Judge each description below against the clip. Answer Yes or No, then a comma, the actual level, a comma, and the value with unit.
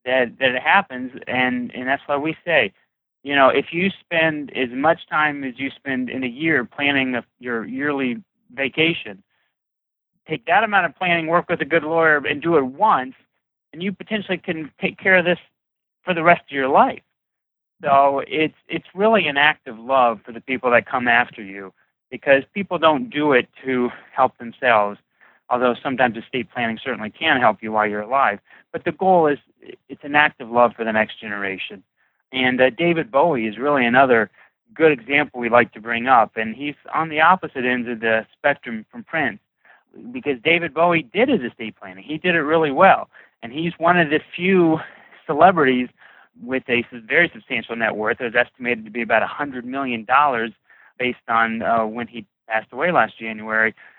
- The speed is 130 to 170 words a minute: No, average, 190 wpm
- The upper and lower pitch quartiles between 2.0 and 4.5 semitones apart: No, wide, 5.4 semitones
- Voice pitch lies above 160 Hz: No, medium, 140 Hz